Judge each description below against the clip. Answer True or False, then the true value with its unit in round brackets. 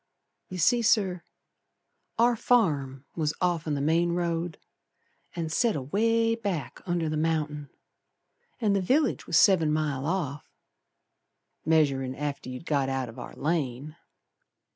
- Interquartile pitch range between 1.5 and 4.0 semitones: False (4.7 semitones)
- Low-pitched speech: False (160 Hz)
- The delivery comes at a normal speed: False (130 wpm)